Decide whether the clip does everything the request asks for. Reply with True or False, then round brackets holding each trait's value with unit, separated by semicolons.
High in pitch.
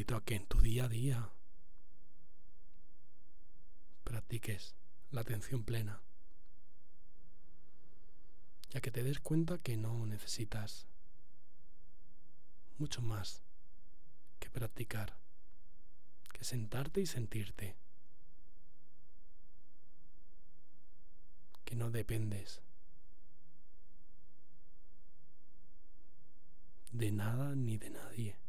False (115 Hz)